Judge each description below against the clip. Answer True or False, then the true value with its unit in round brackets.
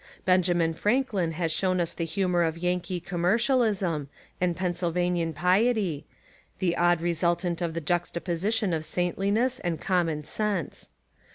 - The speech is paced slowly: False (150 wpm)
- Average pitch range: False (2.3 semitones)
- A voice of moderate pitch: True (175 Hz)